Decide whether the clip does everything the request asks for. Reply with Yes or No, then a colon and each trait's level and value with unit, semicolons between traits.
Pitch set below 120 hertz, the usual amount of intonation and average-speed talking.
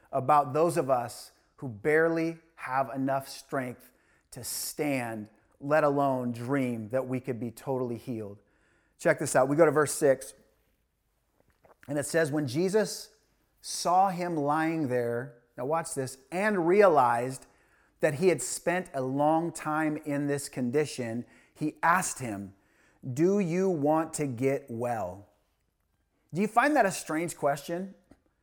No: medium, 140 Hz; average, 4.7 semitones; average, 145 wpm